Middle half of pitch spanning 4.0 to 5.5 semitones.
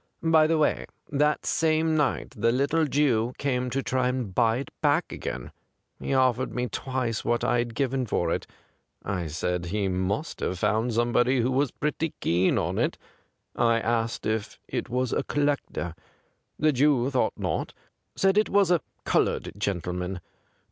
Yes: average, 4.8 semitones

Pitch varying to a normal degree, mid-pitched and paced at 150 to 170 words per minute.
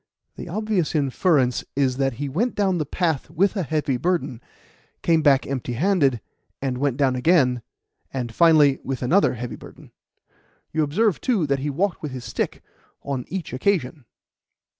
Yes: average, 5.0 semitones; medium, 145 Hz; average, 160 wpm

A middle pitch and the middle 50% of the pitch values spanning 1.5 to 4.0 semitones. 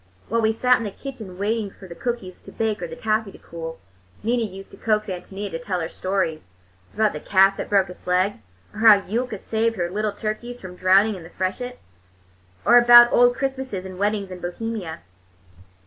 No: high, 205 Hz; average, 3.5 semitones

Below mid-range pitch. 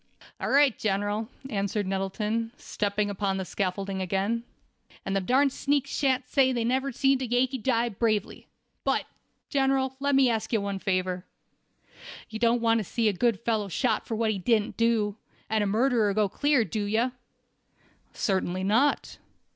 No: high, 220 Hz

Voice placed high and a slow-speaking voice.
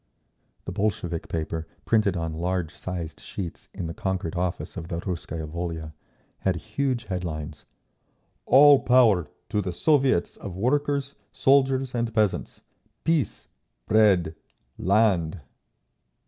No: very low, 95 Hz; slow, 120 wpm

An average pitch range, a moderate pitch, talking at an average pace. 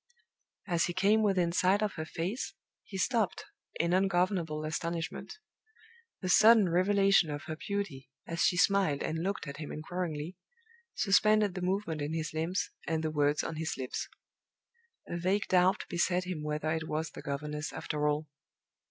Yes: average, 3.8 semitones; medium, 175 Hz; average, 160 wpm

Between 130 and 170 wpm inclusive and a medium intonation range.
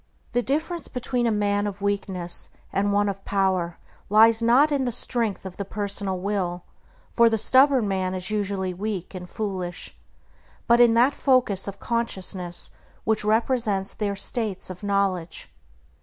Yes: average, 155 wpm; average, 3.5 semitones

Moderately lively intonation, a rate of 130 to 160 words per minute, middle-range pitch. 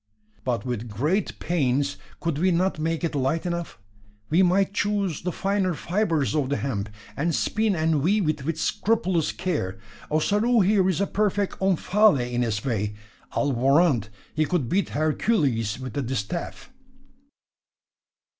No: wide, 6.2 semitones; average, 150 wpm; medium, 160 Hz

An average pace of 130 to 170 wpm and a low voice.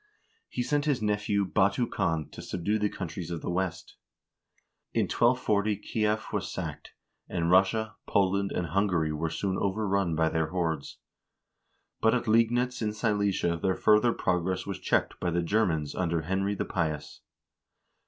Yes: average, 155 wpm; very low, 95 Hz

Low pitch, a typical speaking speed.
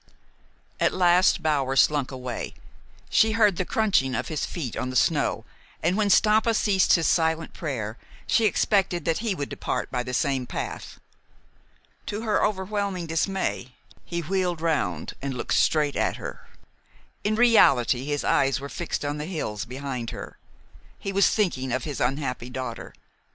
No: medium, 155 Hz; average, 160 wpm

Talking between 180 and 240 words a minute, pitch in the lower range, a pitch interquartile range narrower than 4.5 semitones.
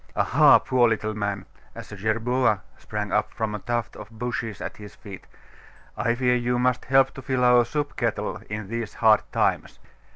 Yes: average, 185 wpm; low, 115 Hz; average, 2.7 semitones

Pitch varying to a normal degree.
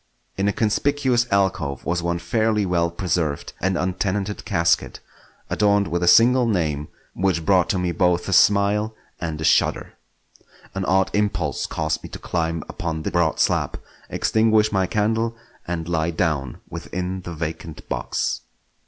Yes: average, 3.6 semitones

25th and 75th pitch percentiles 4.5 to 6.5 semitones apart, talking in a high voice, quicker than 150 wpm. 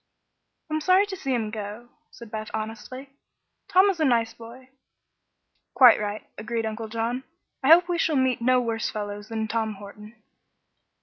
No: average, 3.3 semitones; high, 230 Hz; average, 165 wpm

